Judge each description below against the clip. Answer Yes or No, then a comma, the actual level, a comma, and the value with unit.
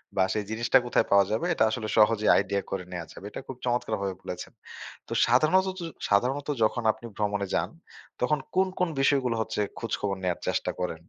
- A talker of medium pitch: No, low, 110 Hz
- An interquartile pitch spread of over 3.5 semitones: Yes, average, 4.3 semitones